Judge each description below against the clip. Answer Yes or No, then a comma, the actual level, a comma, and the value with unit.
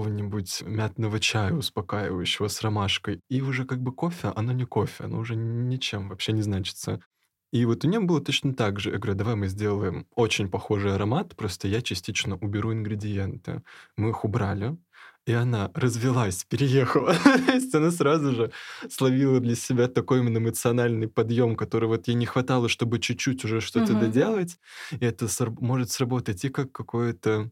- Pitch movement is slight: No, average, 3.3 semitones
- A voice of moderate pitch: No, low, 115 Hz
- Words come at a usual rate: No, fast, 165 wpm